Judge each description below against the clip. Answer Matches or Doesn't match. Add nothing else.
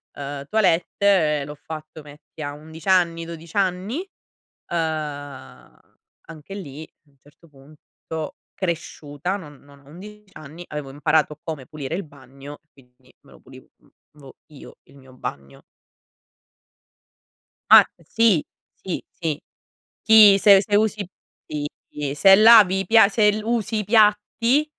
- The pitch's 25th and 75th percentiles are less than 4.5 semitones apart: Doesn't match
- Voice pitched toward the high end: Doesn't match